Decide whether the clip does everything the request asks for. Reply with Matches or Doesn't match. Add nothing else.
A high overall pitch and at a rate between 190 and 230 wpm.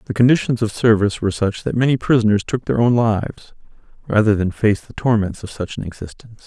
Doesn't match